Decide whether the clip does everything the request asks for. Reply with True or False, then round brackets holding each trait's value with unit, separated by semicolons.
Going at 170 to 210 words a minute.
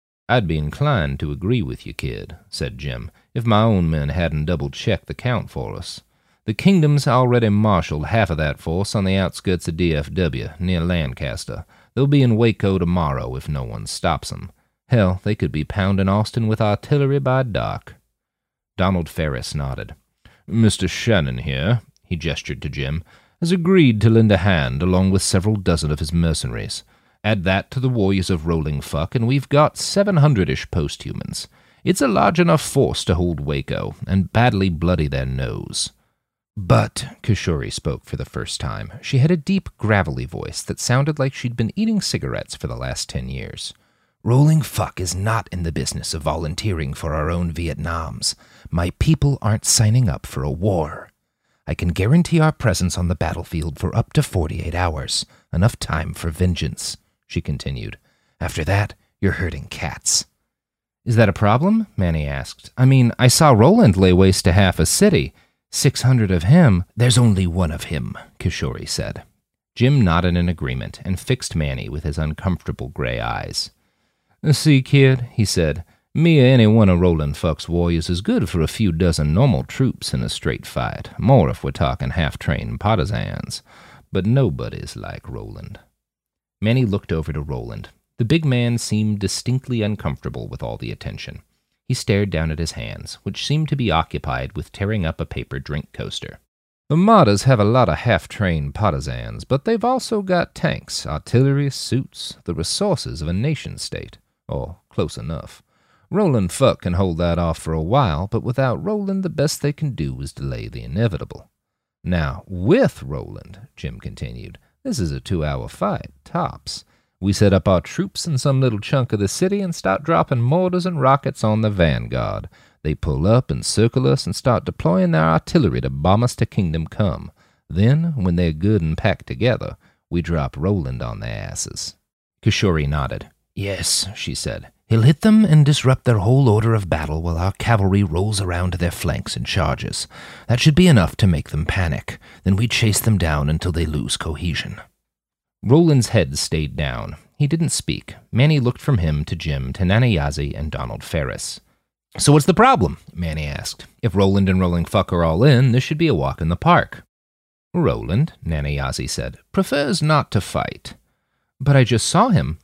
True (180 wpm)